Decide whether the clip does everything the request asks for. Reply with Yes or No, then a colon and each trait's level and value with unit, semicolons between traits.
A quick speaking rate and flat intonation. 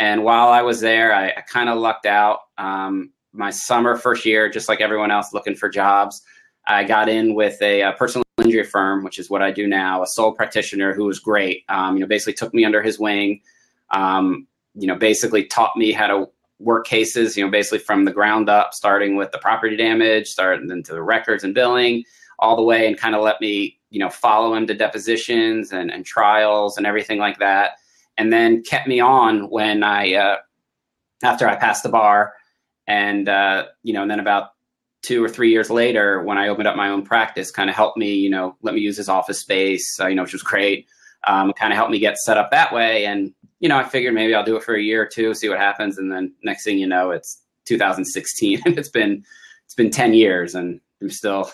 Yes: fast, 230 wpm; narrow, 2.2 semitones